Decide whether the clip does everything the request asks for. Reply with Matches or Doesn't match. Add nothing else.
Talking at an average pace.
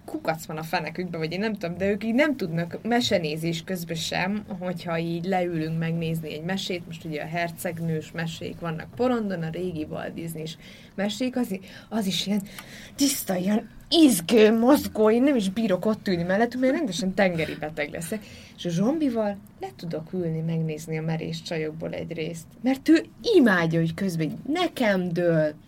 Doesn't match